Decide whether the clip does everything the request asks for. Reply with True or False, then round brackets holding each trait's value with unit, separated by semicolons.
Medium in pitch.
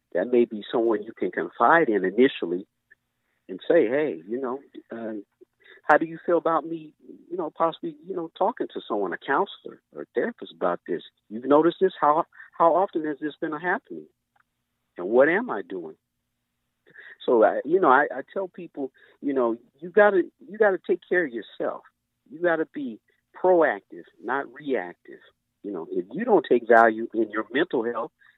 True (170 Hz)